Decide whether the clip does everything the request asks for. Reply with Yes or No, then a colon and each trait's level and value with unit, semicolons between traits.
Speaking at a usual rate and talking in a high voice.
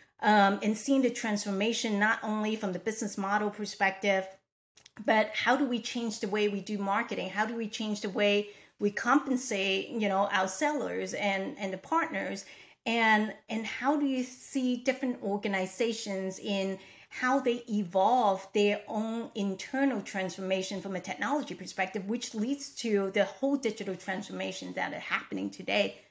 Yes: average, 160 wpm; high, 210 Hz